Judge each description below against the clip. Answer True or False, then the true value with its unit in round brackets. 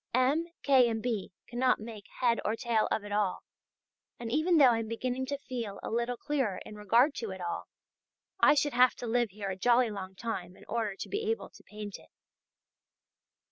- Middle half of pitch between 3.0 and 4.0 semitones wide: True (3.4 semitones)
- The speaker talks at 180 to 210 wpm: True (205 wpm)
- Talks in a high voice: True (235 Hz)